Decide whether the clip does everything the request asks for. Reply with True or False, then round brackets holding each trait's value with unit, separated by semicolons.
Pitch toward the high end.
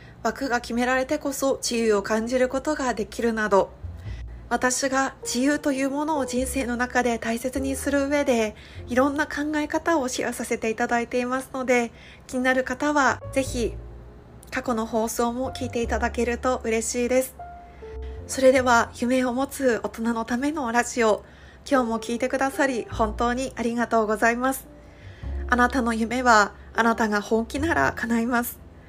True (240 Hz)